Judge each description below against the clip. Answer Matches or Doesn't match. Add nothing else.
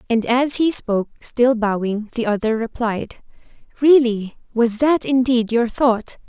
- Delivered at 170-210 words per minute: Doesn't match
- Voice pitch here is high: Matches